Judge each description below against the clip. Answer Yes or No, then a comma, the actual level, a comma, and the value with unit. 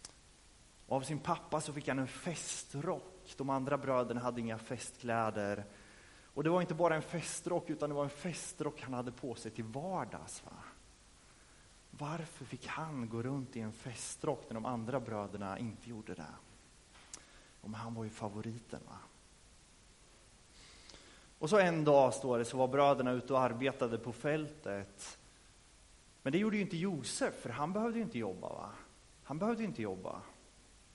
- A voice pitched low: Yes, low, 130 Hz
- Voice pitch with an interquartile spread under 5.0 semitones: No, average, 5.3 semitones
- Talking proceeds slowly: No, average, 170 wpm